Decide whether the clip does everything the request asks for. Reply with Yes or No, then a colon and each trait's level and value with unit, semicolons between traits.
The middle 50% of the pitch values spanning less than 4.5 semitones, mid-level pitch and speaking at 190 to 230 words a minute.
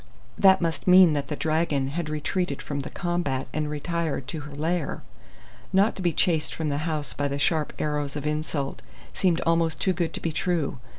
Yes: average, 3.0 semitones; medium, 155 Hz; average, 195 wpm